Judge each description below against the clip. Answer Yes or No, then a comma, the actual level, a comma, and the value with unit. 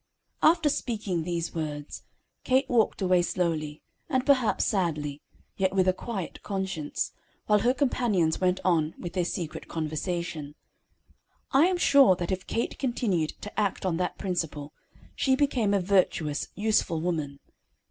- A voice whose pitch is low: No, medium, 185 Hz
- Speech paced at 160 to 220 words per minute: No, average, 145 wpm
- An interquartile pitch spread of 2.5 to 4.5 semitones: No, average, 5.2 semitones